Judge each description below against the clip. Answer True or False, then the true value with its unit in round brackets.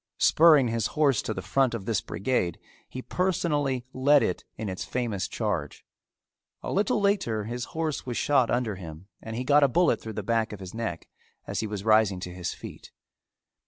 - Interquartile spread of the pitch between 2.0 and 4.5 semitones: False (5.3 semitones)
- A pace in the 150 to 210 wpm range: True (195 wpm)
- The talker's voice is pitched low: True (115 Hz)